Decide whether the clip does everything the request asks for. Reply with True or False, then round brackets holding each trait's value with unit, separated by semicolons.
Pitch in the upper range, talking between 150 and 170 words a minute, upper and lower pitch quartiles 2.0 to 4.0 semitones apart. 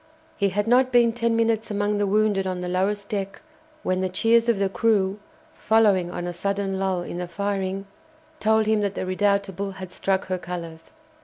False (200 Hz; 190 wpm; 2.5 semitones)